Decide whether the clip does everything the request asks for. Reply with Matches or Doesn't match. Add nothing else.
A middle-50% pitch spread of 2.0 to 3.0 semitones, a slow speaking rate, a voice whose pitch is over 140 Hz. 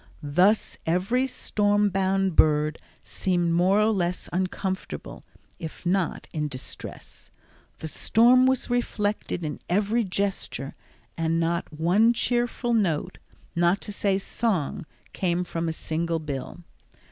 Doesn't match